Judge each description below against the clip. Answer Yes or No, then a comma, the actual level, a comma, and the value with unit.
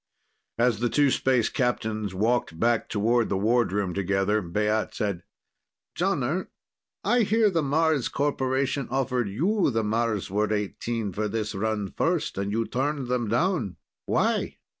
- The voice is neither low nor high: No, low, 115 Hz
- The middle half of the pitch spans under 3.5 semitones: No, average, 4.5 semitones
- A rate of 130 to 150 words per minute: Yes, average, 140 wpm